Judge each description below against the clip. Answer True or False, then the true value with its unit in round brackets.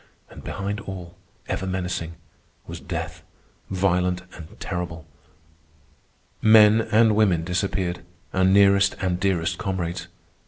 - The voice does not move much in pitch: True (2.0 semitones)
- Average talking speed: False (110 wpm)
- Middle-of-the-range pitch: False (95 Hz)